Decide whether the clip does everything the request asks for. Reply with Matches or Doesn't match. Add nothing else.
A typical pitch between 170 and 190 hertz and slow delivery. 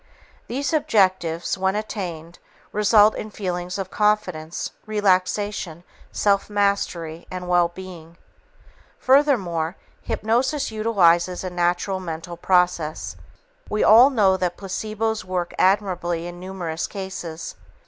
Matches